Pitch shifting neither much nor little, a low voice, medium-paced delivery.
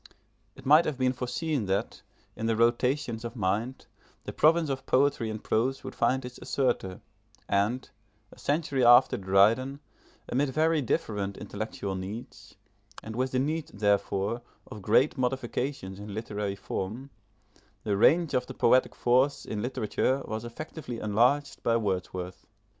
Yes: average, 4.3 semitones; low, 120 Hz; average, 145 wpm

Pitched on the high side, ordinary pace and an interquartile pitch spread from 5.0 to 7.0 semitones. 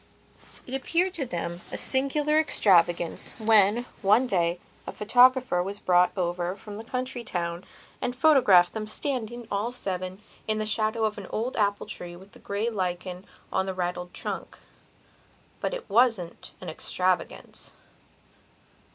Yes: high, 205 Hz; average, 145 wpm; average, 5.3 semitones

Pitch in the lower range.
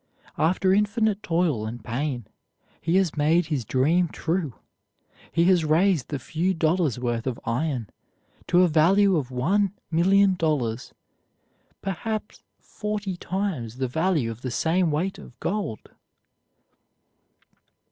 No: medium, 165 Hz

